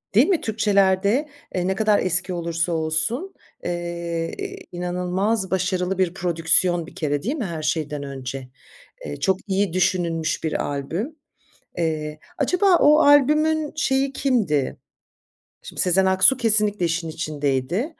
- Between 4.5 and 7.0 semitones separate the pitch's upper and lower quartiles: Yes, wide, 5.6 semitones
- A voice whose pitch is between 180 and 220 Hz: Yes, medium, 185 Hz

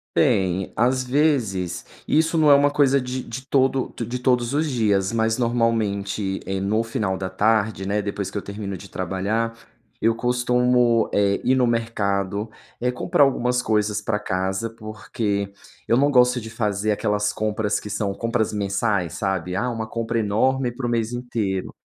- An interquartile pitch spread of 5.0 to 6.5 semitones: No, average, 3.6 semitones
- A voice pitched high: No, low, 110 Hz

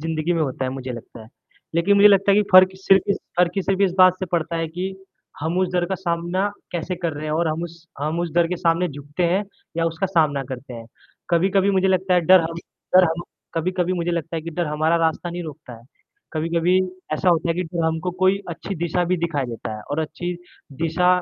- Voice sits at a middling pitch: Yes, medium, 170 Hz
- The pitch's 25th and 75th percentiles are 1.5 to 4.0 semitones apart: Yes, narrow, 2.5 semitones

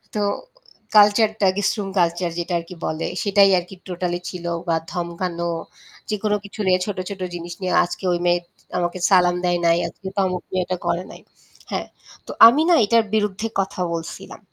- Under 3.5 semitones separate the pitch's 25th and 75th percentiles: Yes, average, 2.7 semitones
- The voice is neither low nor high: Yes, medium, 180 Hz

